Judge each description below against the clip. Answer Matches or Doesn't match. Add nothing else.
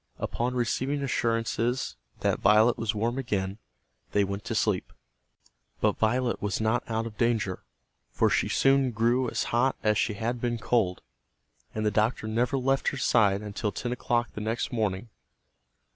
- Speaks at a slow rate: Doesn't match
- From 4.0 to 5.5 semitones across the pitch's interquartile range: Doesn't match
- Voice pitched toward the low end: Matches